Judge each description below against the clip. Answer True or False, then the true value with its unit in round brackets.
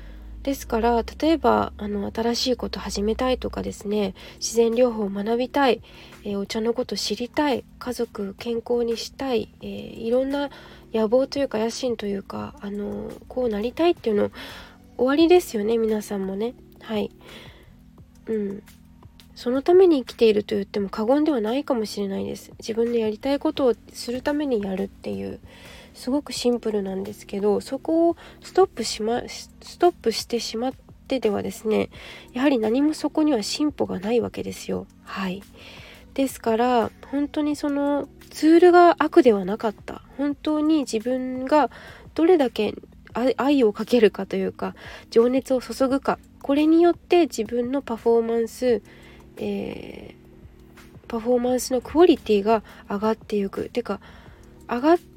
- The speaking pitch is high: True (235 Hz)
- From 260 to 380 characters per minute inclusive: True (325 characters per minute)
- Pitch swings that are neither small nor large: True (4.4 semitones)